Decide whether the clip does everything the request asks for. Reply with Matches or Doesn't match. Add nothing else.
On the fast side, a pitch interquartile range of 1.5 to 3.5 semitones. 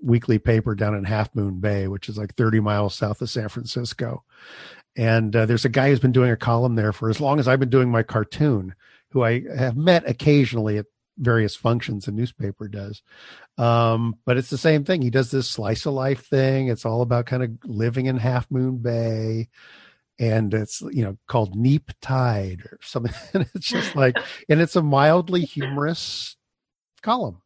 Doesn't match